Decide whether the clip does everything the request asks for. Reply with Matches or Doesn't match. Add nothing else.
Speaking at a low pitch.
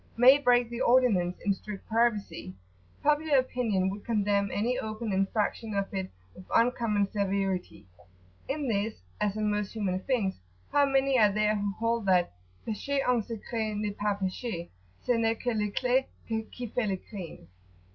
Doesn't match